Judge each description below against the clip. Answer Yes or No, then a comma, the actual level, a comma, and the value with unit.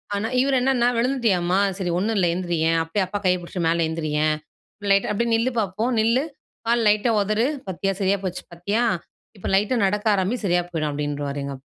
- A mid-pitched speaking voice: No, high, 195 Hz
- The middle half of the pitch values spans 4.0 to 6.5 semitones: Yes, average, 4.7 semitones